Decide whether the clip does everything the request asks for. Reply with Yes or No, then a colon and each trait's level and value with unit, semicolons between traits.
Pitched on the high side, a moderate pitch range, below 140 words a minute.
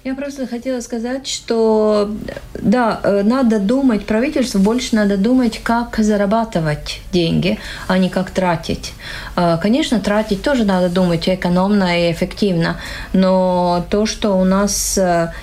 Yes: high, 205 Hz; average, 4.1 semitones; average, 125 wpm